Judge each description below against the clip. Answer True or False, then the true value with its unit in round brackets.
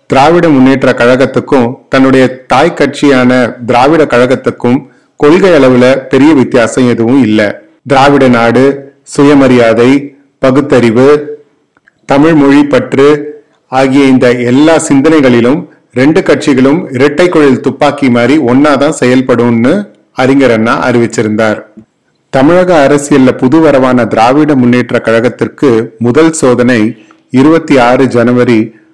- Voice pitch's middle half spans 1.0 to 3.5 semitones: True (2.9 semitones)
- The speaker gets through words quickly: False (95 wpm)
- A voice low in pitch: True (130 Hz)